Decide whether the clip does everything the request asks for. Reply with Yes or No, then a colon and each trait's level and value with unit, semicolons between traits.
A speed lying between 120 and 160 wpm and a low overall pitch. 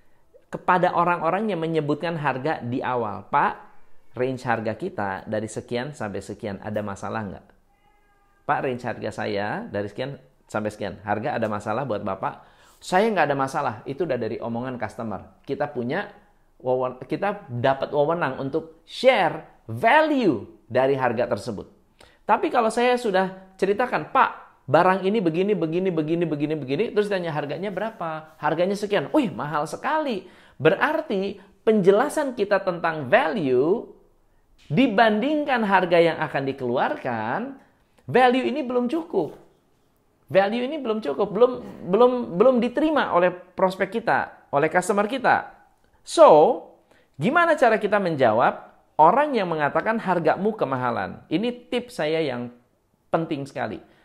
No: average, 130 wpm; medium, 175 Hz